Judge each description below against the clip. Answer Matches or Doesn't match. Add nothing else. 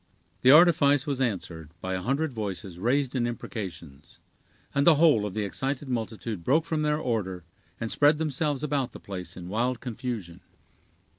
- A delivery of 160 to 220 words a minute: Matches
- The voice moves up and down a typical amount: Doesn't match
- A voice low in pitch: Matches